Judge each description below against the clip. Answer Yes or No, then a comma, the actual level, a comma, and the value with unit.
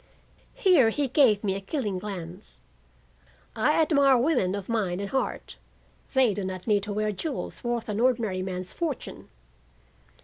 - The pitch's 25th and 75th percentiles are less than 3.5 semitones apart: No, average, 5.3 semitones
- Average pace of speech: Yes, average, 150 wpm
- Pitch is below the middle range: No, high, 215 Hz